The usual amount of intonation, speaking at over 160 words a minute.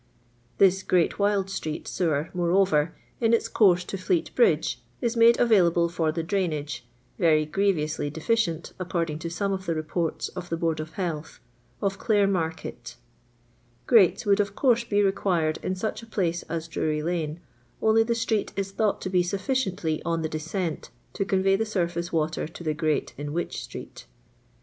Yes: average, 3.7 semitones; average, 170 wpm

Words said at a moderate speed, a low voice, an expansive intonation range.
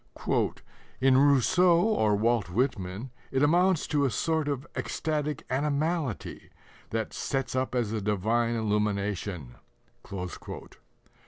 No: slow, 105 wpm; low, 130 Hz; wide, 5.7 semitones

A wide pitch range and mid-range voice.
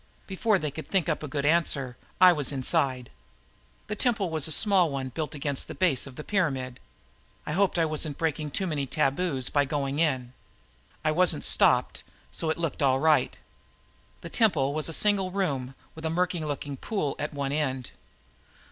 No: average, 4.1 semitones; medium, 150 Hz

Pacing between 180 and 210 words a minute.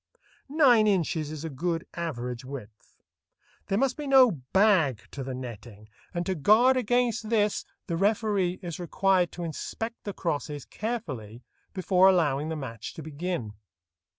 No: average, 150 wpm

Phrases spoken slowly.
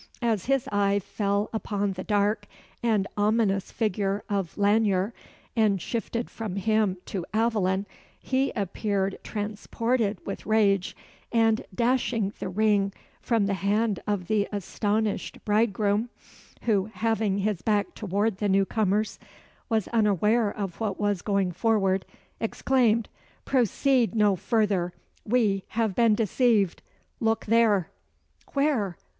Yes: slow, 120 wpm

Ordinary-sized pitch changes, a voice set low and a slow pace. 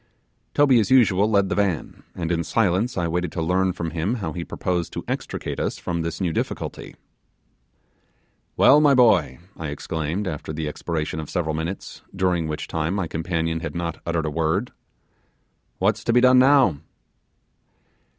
No: average, 3.8 semitones; very low, 85 Hz; average, 170 wpm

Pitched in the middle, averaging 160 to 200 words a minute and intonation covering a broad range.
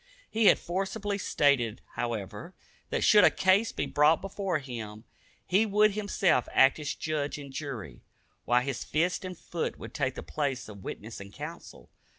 Yes: medium, 150 Hz; average, 165 wpm; wide, 7.7 semitones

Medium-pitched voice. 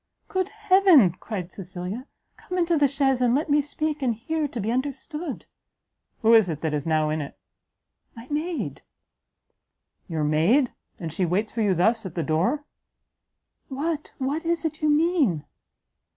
No: very high, 255 Hz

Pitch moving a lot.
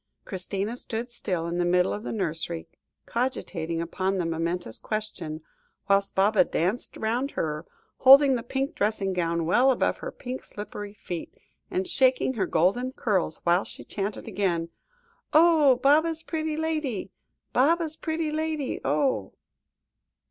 Yes: wide, 7.4 semitones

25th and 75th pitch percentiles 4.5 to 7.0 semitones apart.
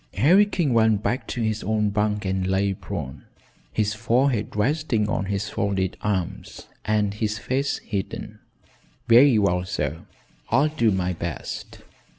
No: average, 3.1 semitones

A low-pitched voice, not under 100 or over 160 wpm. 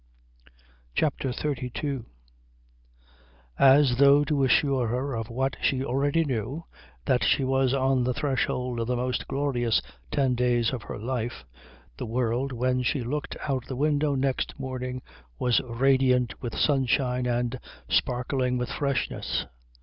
Yes: low, 130 Hz; average, 140 wpm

